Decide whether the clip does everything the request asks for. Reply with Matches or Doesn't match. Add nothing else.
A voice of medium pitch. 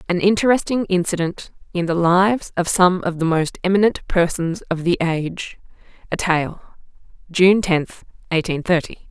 Matches